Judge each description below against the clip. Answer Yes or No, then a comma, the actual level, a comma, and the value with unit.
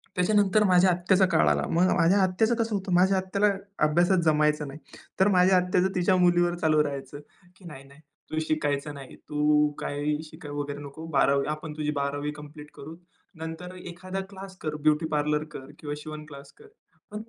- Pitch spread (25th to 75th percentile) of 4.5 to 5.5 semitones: No, average, 3.7 semitones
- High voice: No, medium, 160 Hz